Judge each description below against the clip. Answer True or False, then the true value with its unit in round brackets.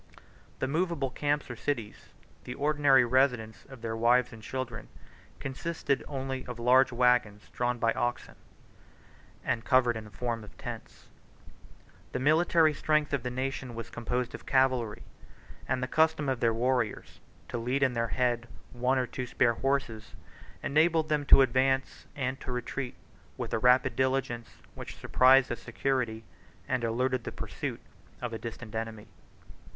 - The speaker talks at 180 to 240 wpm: False (155 wpm)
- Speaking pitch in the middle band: False (125 Hz)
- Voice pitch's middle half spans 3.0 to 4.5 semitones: False (2.4 semitones)